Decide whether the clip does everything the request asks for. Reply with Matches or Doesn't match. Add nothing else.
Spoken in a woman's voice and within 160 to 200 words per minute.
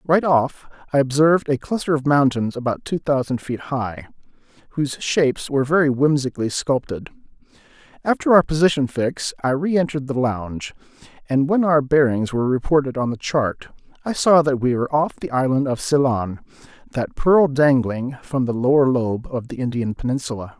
Doesn't match